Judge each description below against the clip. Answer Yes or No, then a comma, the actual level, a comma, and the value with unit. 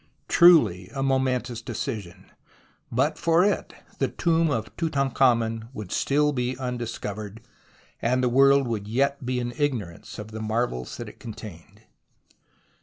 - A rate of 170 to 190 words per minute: No, slow, 135 wpm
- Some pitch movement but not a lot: Yes, average, 3.9 semitones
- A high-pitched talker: No, low, 125 Hz